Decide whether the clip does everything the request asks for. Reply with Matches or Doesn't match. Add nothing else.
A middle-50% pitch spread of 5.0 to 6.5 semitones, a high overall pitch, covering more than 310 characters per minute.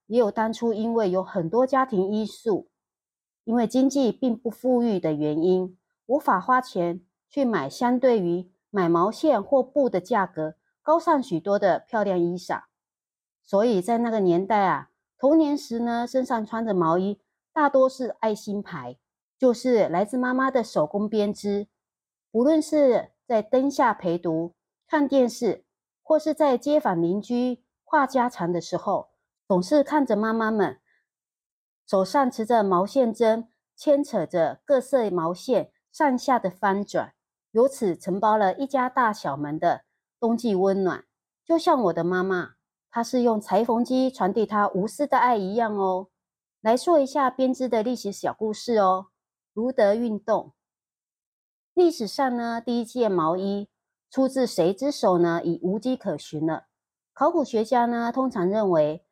Doesn't match